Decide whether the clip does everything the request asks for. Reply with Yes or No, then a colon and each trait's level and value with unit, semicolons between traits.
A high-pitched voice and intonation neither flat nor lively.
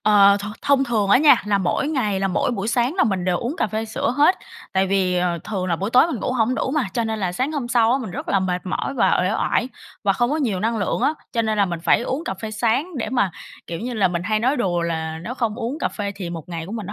Yes: high, 215 Hz; average, 4.8 semitones